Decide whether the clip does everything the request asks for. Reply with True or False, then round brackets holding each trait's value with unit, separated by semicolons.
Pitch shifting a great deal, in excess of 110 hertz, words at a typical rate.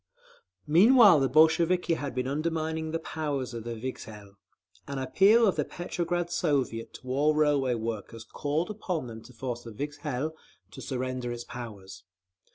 False (5.0 semitones; 140 Hz; 155 wpm)